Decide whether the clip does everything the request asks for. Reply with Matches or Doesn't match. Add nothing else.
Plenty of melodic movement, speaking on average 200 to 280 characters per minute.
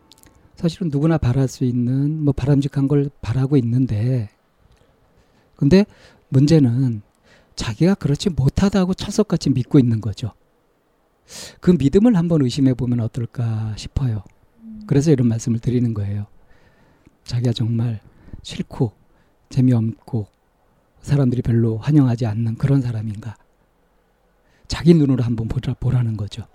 Doesn't match